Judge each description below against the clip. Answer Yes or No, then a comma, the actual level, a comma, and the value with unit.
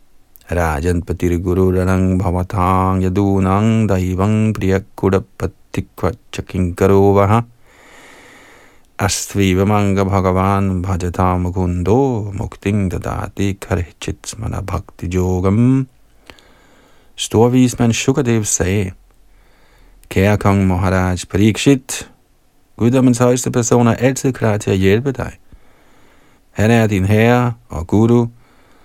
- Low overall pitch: Yes, low, 100 Hz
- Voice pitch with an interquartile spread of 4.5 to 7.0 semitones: No, average, 3.7 semitones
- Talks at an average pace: No, slow, 85 wpm